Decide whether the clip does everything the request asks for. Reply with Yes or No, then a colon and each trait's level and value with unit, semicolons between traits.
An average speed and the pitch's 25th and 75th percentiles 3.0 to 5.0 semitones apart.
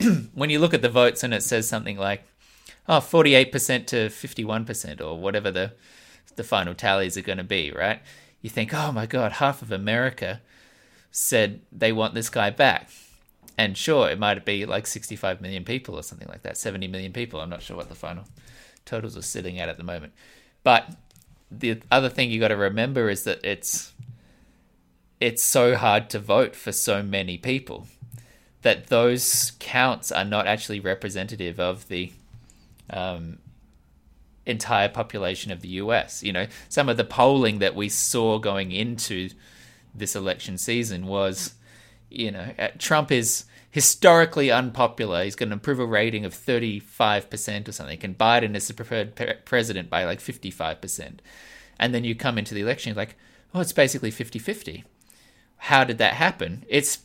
Yes: average, 175 wpm; average, 3.9 semitones